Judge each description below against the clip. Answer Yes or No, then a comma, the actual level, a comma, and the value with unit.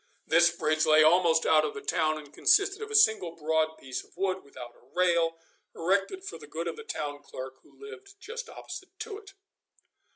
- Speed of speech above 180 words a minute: Yes, average, 200 wpm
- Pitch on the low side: No, medium, 170 Hz